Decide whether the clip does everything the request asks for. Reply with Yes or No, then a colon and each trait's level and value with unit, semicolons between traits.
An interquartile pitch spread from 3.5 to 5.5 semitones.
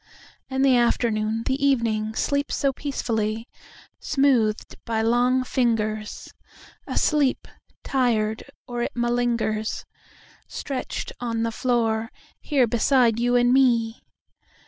No: narrow, 2.6 semitones